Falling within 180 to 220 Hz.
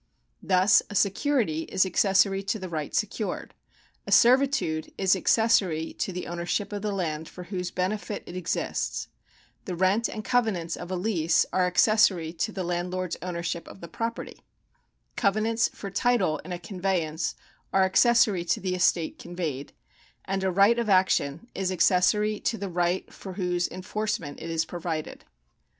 Yes: medium, 185 Hz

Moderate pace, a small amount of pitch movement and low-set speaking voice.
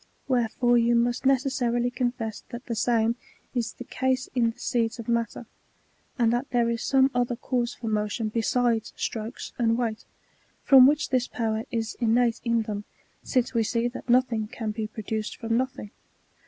No: average, 170 wpm; narrow, 1.7 semitones; high, 235 Hz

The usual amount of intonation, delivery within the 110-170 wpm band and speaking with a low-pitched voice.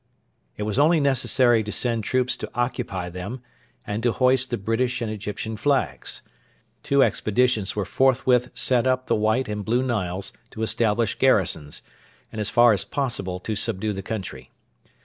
Yes: average, 3.7 semitones; average, 165 wpm; low, 115 Hz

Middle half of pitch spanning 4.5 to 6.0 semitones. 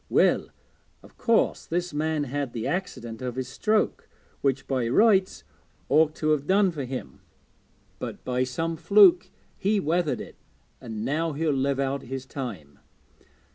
Yes: average, 5.3 semitones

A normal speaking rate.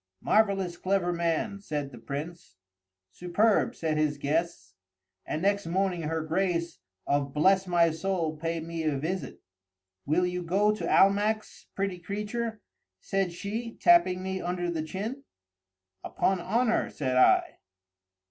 No: slow, 130 wpm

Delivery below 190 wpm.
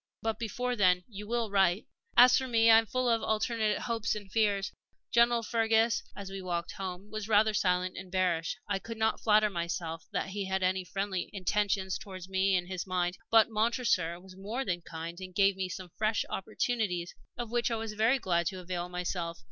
No: average, 200 wpm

